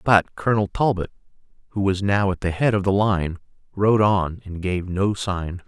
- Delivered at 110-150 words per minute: No, average, 190 wpm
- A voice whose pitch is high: No, very low, 95 Hz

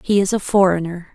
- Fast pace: Yes, fast, 210 wpm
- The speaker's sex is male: No, female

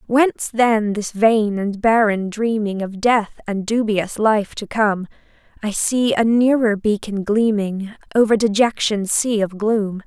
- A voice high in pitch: Yes, high, 215 Hz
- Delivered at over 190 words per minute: No, average, 150 wpm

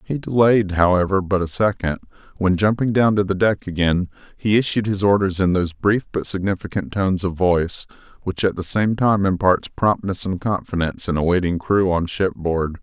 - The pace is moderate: Yes, average, 185 wpm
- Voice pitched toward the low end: Yes, very low, 95 Hz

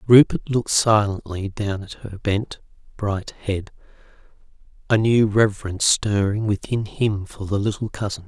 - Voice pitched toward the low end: Yes, low, 105 Hz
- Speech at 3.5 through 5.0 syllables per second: Yes, 4.6 syllables/s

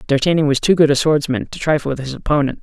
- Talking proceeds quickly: Yes, fast, 250 wpm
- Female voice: No, male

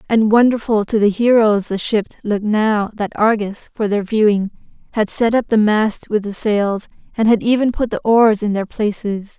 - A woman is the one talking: Yes, female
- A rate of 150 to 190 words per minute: No, average, 200 wpm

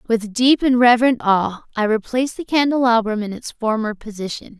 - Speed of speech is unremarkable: Yes, average, 170 wpm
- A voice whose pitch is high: Yes, high, 230 Hz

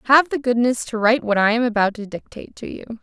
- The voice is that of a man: No, female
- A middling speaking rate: No, fast, 260 wpm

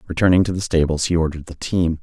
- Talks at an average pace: No, fast, 235 wpm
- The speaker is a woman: No, male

